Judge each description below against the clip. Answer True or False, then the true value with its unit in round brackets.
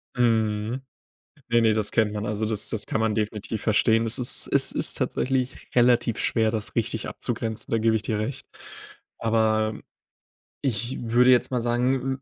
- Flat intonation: True (1.9 semitones)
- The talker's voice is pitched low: True (115 Hz)